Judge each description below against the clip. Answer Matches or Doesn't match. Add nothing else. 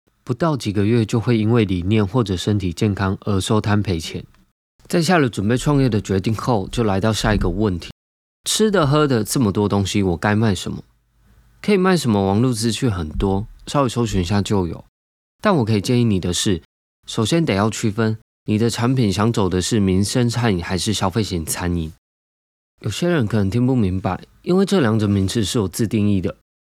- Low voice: Matches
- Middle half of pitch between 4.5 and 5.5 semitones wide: Doesn't match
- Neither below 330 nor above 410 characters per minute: Doesn't match